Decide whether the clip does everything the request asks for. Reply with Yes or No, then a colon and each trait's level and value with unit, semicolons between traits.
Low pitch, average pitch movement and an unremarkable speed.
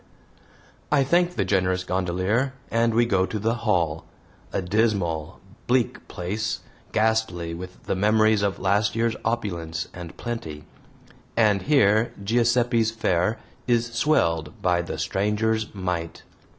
No: low, 105 Hz; average, 4.3 semitones; slow, 125 wpm